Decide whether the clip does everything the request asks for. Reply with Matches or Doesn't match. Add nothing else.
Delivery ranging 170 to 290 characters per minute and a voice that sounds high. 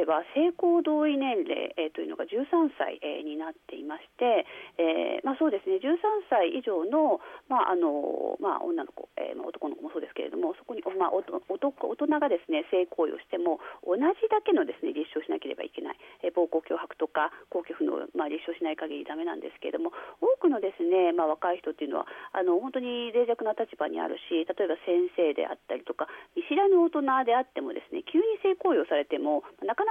Doesn't match